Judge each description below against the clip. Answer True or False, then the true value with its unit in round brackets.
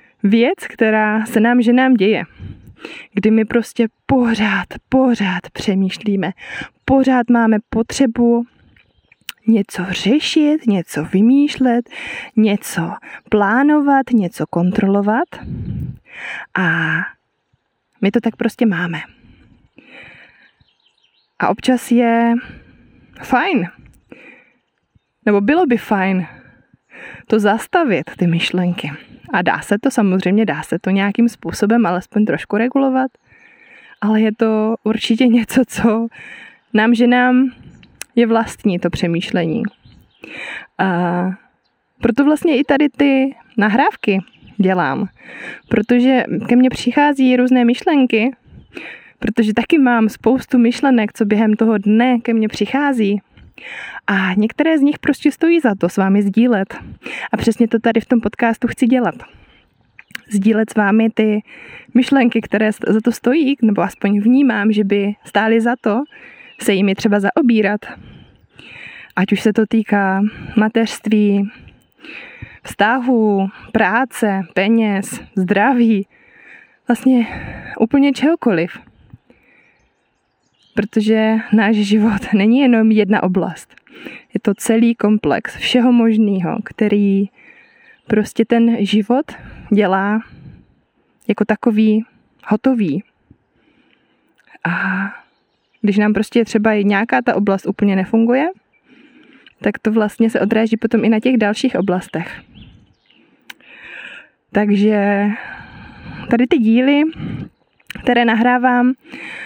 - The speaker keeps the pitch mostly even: False (3.3 semitones)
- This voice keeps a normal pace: False (105 wpm)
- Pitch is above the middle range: True (225 Hz)